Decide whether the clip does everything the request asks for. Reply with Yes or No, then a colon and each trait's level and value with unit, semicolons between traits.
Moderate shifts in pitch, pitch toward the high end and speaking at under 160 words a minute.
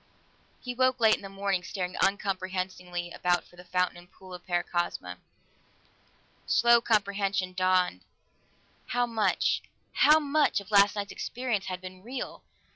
Yes: average, 3.3 semitones; high, 195 Hz; average, 140 wpm